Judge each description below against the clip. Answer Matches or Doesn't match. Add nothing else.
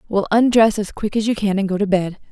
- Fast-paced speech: Matches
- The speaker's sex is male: Doesn't match